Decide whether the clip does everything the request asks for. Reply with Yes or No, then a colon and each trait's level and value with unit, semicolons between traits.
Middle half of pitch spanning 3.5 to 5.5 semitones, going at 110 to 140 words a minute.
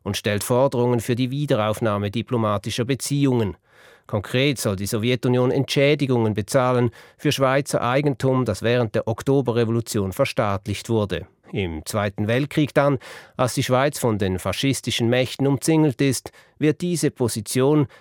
Yes: average, 3.9 semitones; average, 130 wpm